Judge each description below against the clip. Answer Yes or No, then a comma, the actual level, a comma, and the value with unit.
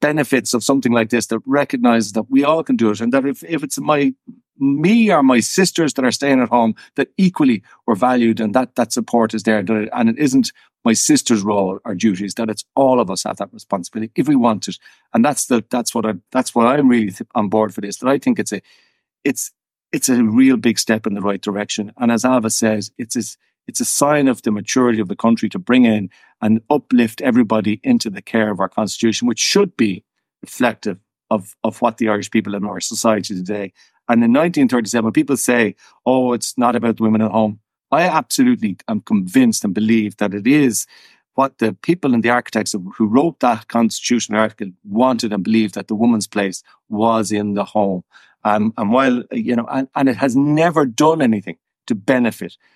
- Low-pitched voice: Yes, low, 115 Hz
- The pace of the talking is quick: Yes, fast, 215 wpm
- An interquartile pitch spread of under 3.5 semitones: No, average, 4.2 semitones